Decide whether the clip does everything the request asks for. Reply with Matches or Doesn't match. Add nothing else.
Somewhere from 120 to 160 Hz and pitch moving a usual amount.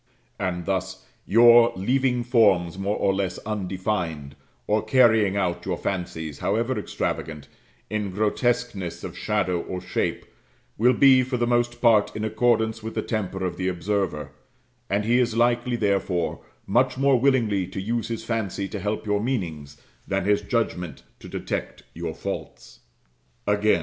Doesn't match